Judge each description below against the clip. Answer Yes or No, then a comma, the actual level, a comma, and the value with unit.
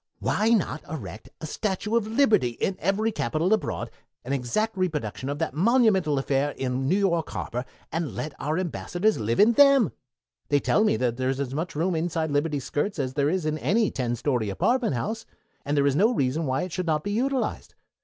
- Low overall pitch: No, medium, 160 Hz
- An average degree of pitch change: No, wide, 7.1 semitones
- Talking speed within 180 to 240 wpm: Yes, average, 200 wpm